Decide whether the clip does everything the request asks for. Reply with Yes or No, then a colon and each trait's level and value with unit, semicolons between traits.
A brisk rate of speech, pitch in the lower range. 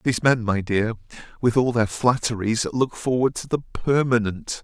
No: average, 170 wpm; low, 120 Hz